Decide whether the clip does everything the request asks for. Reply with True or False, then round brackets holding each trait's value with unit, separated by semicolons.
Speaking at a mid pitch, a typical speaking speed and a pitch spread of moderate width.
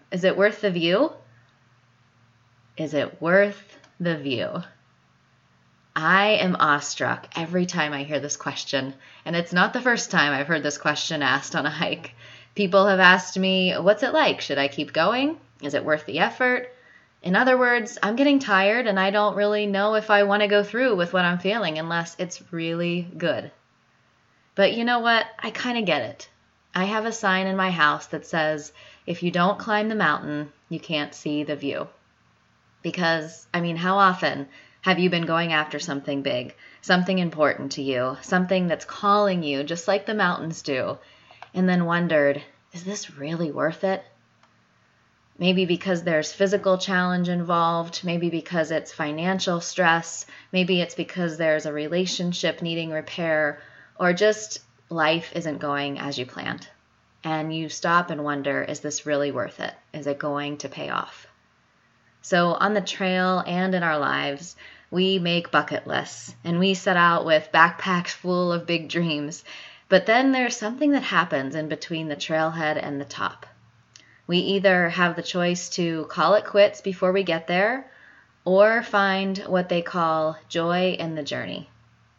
True (170 Hz; 170 wpm; 4.0 semitones)